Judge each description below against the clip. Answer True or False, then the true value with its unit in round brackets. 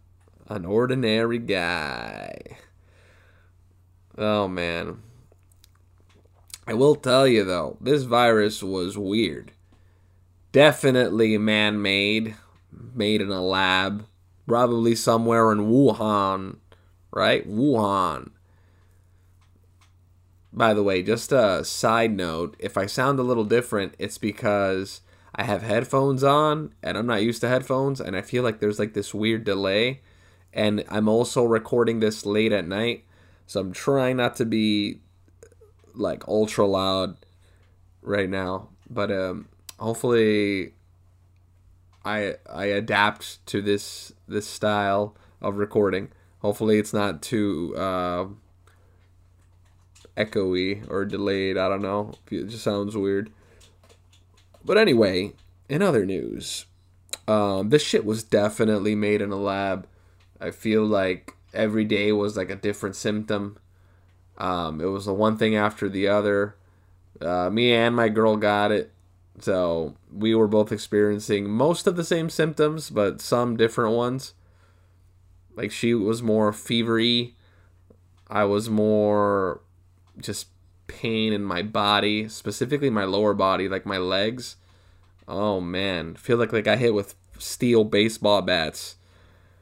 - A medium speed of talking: False (130 wpm)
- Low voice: True (100 Hz)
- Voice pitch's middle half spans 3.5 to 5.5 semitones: False (3.0 semitones)